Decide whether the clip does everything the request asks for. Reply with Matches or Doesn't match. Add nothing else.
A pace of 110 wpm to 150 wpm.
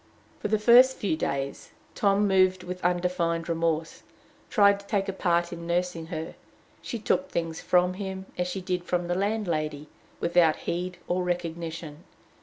Doesn't match